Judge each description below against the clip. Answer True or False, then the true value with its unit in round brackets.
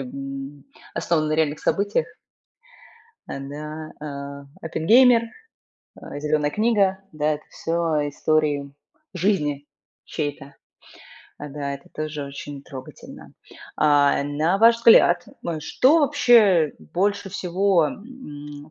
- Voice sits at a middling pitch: True (155 Hz)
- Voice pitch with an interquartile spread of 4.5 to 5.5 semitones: True (4.9 semitones)